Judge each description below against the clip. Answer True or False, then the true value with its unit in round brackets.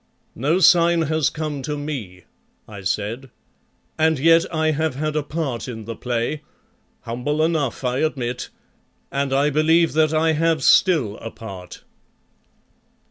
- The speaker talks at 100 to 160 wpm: True (140 wpm)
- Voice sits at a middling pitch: True (150 Hz)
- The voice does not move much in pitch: False (4.5 semitones)